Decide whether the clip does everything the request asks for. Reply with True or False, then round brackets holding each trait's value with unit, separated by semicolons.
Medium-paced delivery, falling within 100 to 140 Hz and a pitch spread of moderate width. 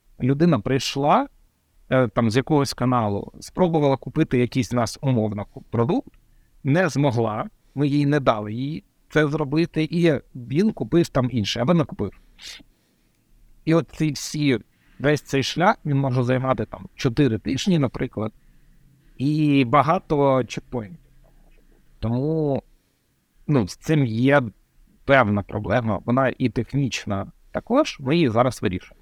True (125 wpm; 135 Hz; 4.1 semitones)